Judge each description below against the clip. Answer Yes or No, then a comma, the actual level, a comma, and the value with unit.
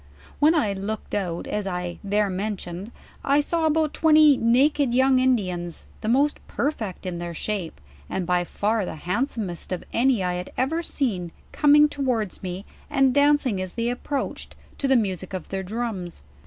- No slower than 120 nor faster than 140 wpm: No, average, 180 wpm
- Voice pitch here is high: Yes, high, 220 Hz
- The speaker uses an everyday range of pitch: No, wide, 6.8 semitones